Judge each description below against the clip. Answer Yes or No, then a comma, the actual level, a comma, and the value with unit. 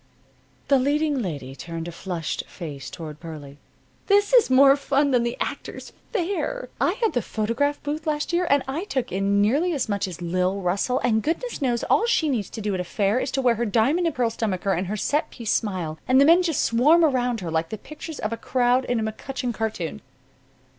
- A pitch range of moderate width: No, wide, 7.0 semitones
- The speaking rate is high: Yes, fast, 215 wpm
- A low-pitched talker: No, high, 240 Hz